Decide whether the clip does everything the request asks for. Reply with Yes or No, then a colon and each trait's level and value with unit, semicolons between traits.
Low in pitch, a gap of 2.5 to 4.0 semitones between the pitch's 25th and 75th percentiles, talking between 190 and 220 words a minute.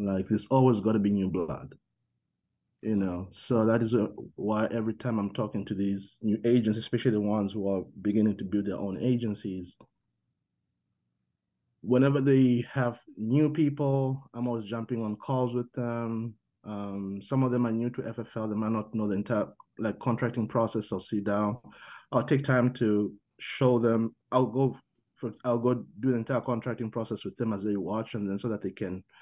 Yes: low, 115 Hz; average, 2.8 semitones; average, 195 wpm